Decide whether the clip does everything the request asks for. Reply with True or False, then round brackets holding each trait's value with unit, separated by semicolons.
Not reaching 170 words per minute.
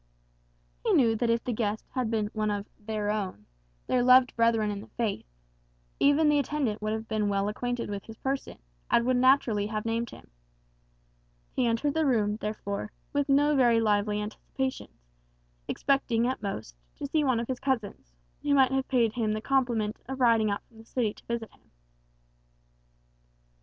False (180 wpm)